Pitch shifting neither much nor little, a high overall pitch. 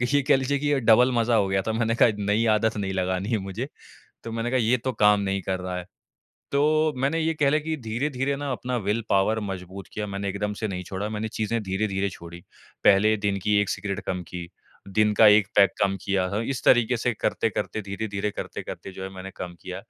No: average, 3.6 semitones; low, 105 Hz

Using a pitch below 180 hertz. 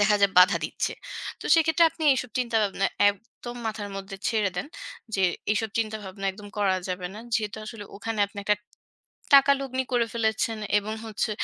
No: high, 215 Hz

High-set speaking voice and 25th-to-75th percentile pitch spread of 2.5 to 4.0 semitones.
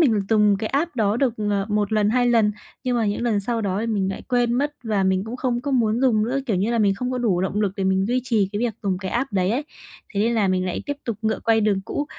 Yes: high, 220 Hz; average, 3.4 semitones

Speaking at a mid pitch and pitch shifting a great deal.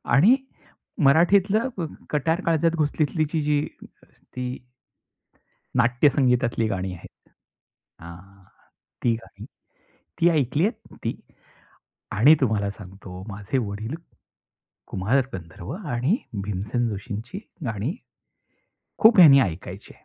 No: low, 125 Hz; wide, 7.6 semitones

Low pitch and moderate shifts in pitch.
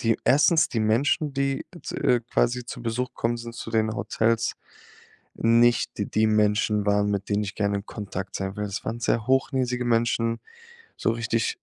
No: low, 115 Hz; narrow, 2.3 semitones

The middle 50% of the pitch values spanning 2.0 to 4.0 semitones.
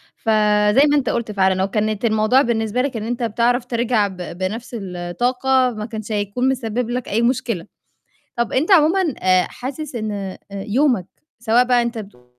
Yes: average, 3.4 semitones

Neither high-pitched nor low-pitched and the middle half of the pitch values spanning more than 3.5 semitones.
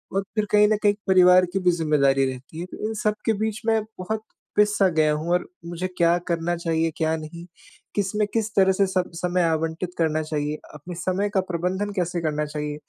Yes: medium, 175 Hz; average, 4.2 semitones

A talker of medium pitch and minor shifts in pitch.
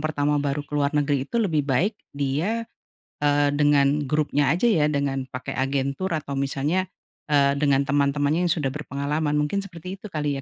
Yes: medium, 145 Hz; narrow, 2.0 semitones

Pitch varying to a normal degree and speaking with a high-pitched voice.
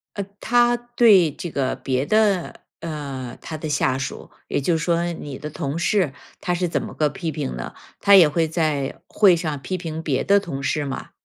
No: average, 4.7 semitones; medium, 160 Hz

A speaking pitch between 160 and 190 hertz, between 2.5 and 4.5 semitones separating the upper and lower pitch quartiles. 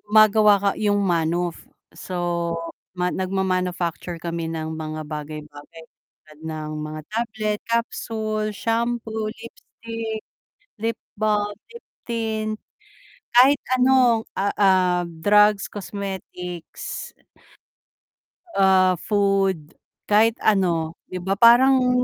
No: high, 200 Hz; average, 4.2 semitones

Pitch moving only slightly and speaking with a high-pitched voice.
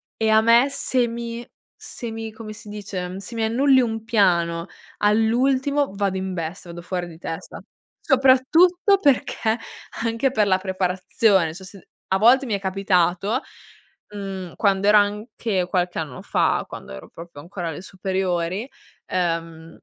No: average, 4.3 semitones; high, 200 Hz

